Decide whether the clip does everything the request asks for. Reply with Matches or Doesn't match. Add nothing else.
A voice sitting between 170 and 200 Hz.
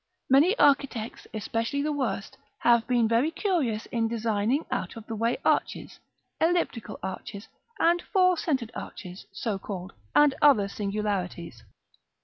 Doesn't match